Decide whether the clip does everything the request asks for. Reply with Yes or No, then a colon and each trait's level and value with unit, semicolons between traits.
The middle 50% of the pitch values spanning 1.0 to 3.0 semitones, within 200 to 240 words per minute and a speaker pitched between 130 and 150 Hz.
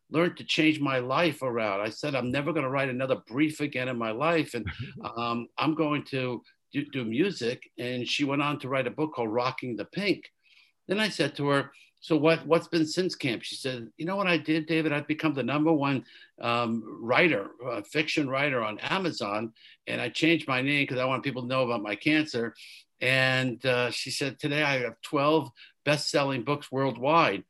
No: average, 3.6 semitones; fast, 205 wpm; medium, 140 Hz